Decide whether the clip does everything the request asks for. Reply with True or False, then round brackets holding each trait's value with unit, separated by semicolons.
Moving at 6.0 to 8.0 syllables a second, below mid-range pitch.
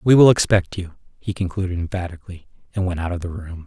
True (6.4 syllables/s; 90 Hz)